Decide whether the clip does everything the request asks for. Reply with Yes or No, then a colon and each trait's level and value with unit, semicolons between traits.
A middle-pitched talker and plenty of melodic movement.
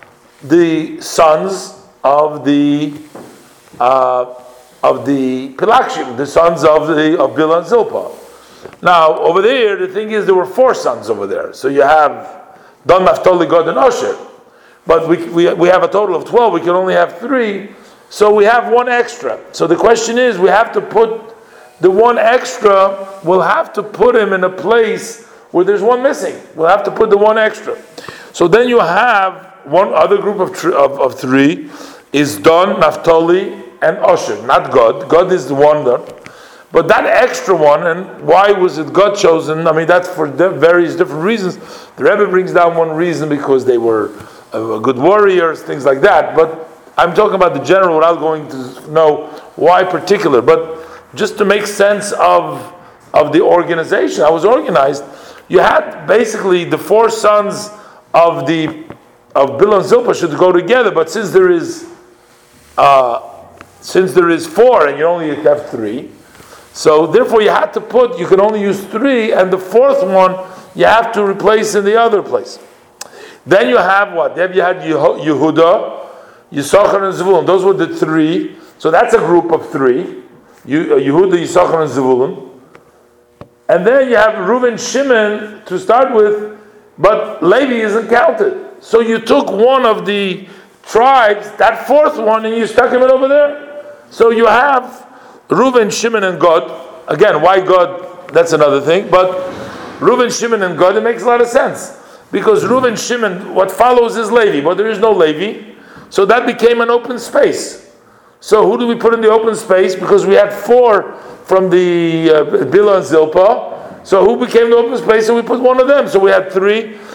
No: high, 210 Hz; wide, 6.3 semitones